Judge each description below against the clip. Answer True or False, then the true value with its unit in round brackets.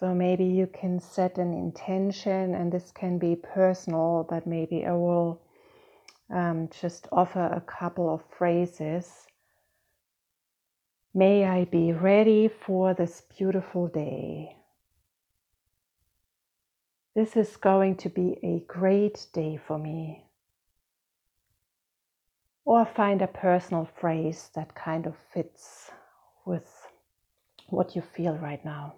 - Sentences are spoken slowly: True (115 wpm)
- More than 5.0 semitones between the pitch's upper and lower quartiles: False (3.4 semitones)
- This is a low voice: False (175 Hz)